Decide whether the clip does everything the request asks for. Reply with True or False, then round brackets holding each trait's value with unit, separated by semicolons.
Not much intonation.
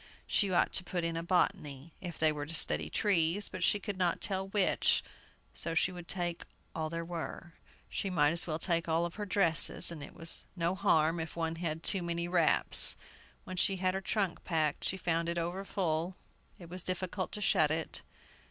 True (2.2 semitones)